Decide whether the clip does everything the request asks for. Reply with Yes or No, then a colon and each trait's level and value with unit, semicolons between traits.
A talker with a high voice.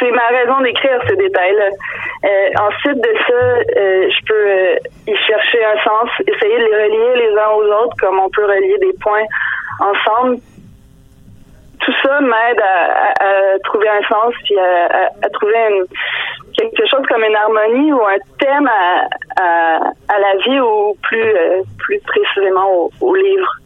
Yes: high, 245 Hz